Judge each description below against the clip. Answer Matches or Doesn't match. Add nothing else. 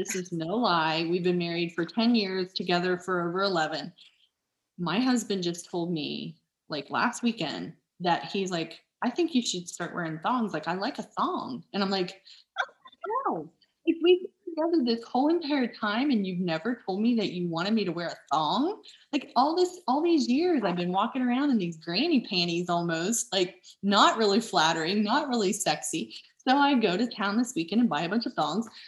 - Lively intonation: Matches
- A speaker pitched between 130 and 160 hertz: Doesn't match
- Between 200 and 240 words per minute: Matches